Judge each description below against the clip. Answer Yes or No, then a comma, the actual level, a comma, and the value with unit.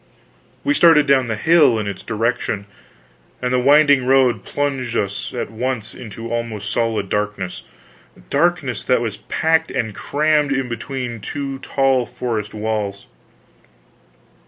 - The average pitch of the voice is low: Yes, low, 120 Hz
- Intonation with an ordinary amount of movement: Yes, average, 4.1 semitones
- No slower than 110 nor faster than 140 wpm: Yes, slow, 135 wpm